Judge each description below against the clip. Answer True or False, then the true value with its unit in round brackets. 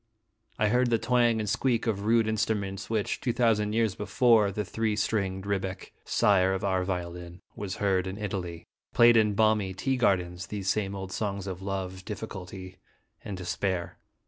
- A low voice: True (100 Hz)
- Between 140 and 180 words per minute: True (170 wpm)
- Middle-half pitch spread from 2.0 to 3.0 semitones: True (2.7 semitones)